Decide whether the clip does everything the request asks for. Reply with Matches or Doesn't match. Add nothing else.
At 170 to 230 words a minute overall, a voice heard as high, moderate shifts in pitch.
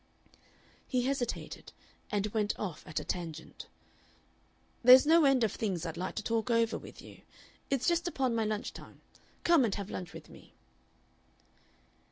Doesn't match